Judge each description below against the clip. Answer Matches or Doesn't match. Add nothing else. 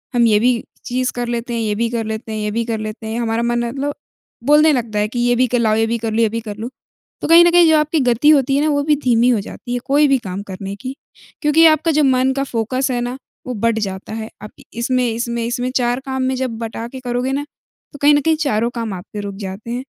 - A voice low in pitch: Doesn't match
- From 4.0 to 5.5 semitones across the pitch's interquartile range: Doesn't match